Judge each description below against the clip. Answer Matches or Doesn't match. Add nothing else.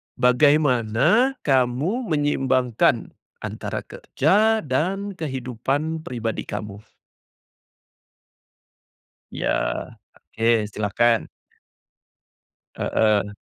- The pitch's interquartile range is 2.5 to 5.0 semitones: Doesn't match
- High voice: Doesn't match